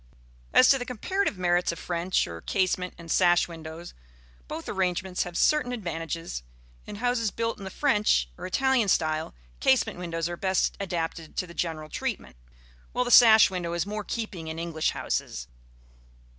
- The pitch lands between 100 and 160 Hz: No, medium, 180 Hz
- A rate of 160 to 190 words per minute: Yes, average, 170 wpm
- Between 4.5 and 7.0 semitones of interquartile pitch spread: Yes, average, 4.9 semitones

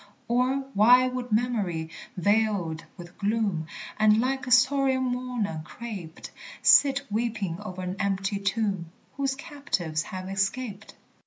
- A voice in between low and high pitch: No, high, 215 Hz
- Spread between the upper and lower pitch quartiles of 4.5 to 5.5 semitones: Yes, average, 4.9 semitones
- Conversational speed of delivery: No, slow, 125 wpm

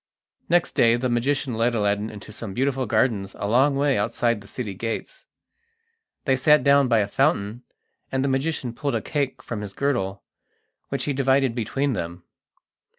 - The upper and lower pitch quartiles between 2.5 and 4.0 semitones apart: No, average, 4.4 semitones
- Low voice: Yes, low, 120 Hz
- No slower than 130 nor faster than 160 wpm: No, average, 170 wpm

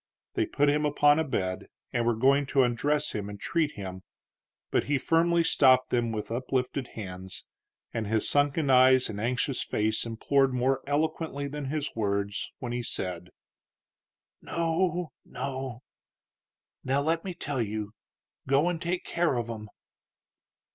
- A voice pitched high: No, low, 130 Hz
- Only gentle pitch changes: No, average, 4.7 semitones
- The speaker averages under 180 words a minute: Yes, average, 150 wpm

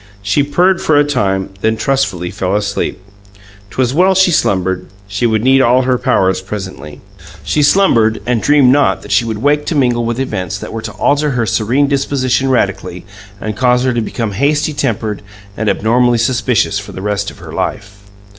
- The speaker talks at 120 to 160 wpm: No, average, 185 wpm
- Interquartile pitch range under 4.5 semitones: No, average, 5.1 semitones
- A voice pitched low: Yes, low, 120 Hz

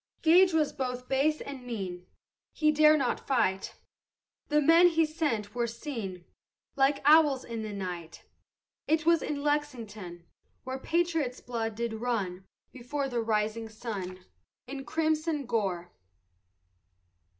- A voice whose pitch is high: Yes, very high, 250 Hz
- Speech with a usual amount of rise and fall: No, wide, 5.9 semitones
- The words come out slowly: Yes, slow, 125 wpm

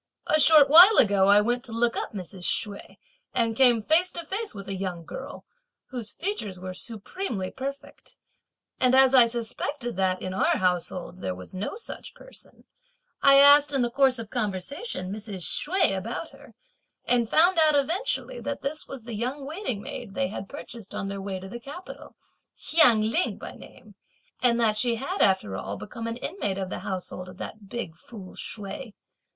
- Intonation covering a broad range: Yes, wide, 6.3 semitones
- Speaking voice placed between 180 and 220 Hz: No, high, 230 Hz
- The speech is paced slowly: No, average, 185 wpm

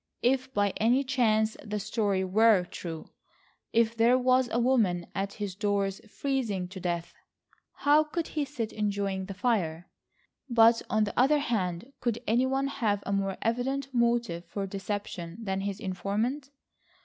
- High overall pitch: Yes, high, 215 Hz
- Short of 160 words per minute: Yes, average, 150 wpm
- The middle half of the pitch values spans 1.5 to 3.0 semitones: No, average, 4.2 semitones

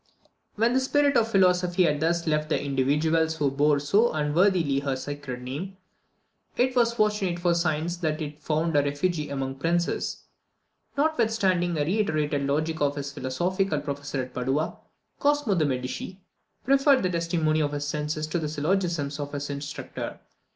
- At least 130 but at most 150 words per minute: No, average, 160 wpm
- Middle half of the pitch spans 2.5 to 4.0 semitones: No, average, 4.4 semitones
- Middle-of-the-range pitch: Yes, medium, 155 Hz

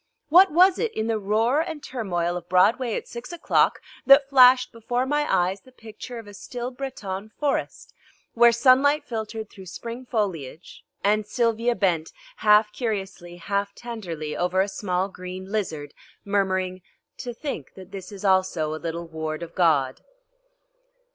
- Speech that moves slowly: No, average, 155 wpm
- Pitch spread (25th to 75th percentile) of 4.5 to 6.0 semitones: Yes, average, 5.1 semitones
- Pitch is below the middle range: No, high, 210 Hz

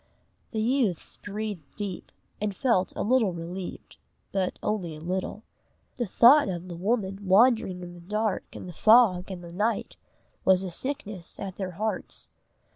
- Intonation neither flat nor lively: Yes, average, 3.3 semitones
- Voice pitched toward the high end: Yes, high, 195 Hz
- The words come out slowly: No, average, 160 wpm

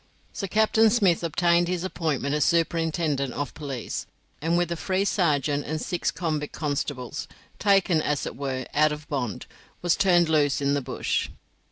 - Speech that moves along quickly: No, average, 165 wpm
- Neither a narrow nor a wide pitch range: Yes, average, 3.5 semitones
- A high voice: No, medium, 160 Hz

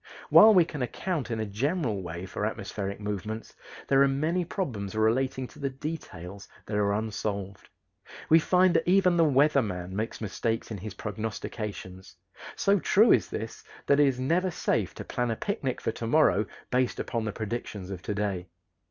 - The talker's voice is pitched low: Yes, low, 115 Hz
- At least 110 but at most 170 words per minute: No, average, 180 wpm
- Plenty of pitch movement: Yes, wide, 6.6 semitones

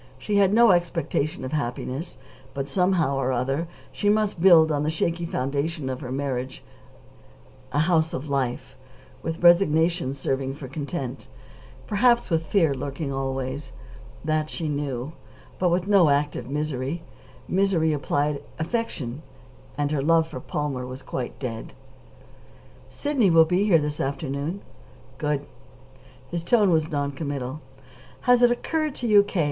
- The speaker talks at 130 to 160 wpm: Yes, average, 145 wpm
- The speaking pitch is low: No, medium, 155 Hz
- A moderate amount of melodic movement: Yes, average, 4.1 semitones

